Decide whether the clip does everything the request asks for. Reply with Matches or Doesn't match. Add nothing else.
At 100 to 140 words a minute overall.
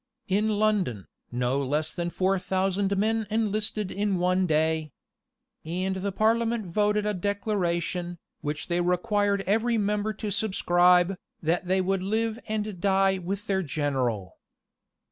Matches